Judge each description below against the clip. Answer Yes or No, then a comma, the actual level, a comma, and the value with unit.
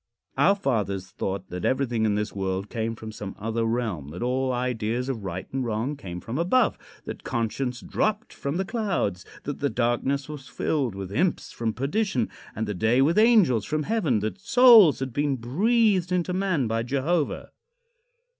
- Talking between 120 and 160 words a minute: No, average, 175 wpm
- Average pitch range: No, wide, 7.1 semitones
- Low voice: Yes, low, 125 Hz